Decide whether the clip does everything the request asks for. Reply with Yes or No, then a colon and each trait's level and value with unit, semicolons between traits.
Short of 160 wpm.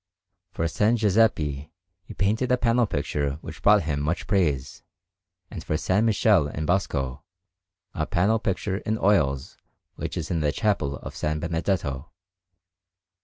Yes: average, 145 wpm